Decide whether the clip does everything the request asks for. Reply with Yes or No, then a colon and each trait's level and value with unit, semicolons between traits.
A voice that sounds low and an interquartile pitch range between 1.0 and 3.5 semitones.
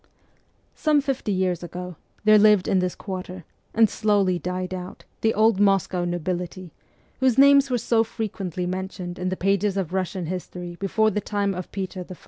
No: high, 190 Hz; average, 2.8 semitones